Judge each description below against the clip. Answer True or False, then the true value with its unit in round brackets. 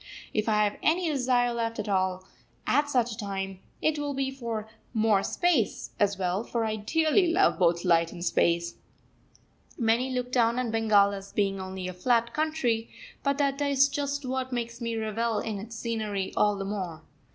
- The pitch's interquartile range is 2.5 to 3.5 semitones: False (4.7 semitones)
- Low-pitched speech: False (225 Hz)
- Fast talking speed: False (185 wpm)